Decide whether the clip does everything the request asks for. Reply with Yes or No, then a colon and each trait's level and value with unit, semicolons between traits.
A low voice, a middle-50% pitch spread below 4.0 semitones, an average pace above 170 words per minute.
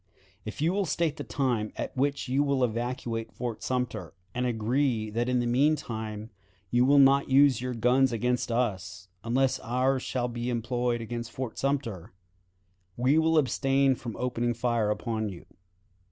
No: low, 125 Hz; average, 2.7 semitones; average, 165 wpm